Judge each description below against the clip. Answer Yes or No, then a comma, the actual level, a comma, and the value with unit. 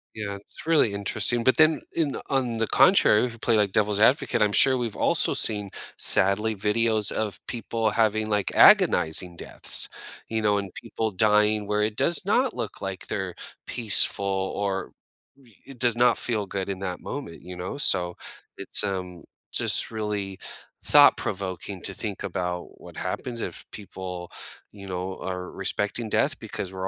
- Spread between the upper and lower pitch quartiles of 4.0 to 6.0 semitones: No, average, 3.1 semitones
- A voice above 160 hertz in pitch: No, low, 105 Hz